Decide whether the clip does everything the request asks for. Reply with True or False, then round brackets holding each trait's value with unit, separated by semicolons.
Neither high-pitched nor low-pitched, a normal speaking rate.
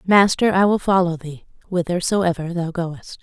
True (175 Hz; 150 wpm)